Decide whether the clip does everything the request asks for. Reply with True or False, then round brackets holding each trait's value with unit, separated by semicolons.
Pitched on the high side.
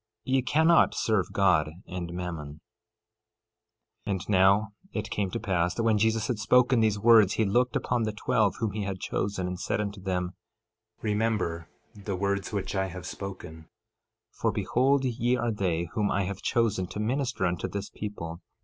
False (100 Hz)